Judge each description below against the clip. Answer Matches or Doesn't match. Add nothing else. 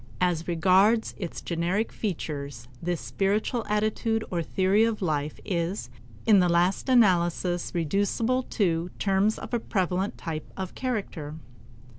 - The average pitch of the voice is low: Doesn't match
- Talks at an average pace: Doesn't match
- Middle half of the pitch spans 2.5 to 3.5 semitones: Doesn't match